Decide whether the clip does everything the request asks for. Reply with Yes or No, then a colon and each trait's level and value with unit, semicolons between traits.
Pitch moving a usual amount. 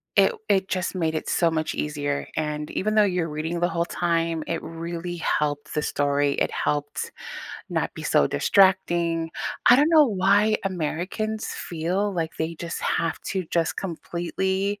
Yes: average, 3.2 semitones